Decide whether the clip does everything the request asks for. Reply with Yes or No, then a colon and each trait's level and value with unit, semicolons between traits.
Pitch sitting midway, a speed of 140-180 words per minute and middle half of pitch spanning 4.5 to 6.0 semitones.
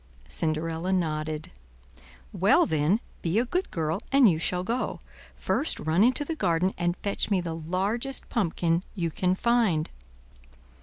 Yes: medium, 180 Hz; average, 145 wpm; average, 5.3 semitones